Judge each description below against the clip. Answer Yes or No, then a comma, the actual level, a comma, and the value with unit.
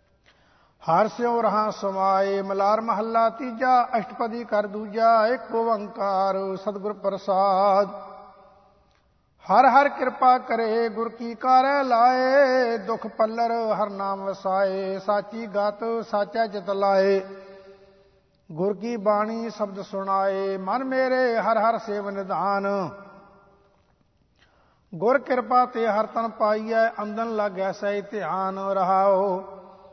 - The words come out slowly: Yes, slow, 110 wpm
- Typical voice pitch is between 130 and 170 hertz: No, high, 210 Hz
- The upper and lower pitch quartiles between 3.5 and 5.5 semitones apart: No, average, 2.7 semitones